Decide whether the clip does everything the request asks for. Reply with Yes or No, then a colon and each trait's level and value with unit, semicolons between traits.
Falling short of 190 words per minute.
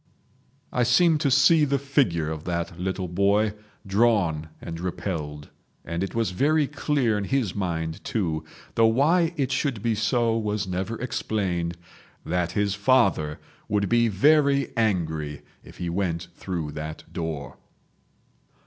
Yes: average, 140 wpm